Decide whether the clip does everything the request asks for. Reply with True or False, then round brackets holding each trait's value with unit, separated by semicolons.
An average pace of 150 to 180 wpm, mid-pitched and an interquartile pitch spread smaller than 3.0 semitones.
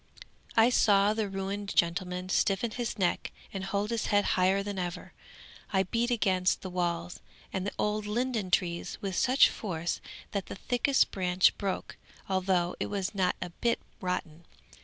False (160 wpm; 195 Hz; 2.5 semitones)